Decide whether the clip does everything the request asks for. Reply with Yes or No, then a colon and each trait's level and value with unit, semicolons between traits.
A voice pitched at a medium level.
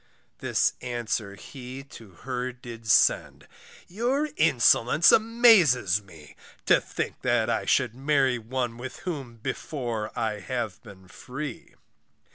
No: low, 125 Hz